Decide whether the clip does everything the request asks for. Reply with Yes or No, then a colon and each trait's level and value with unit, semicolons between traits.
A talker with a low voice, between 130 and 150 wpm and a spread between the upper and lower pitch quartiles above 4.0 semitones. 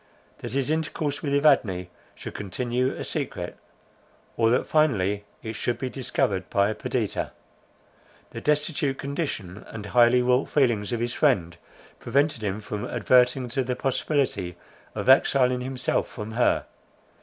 Yes: low, 125 Hz; average, 145 wpm; average, 4.4 semitones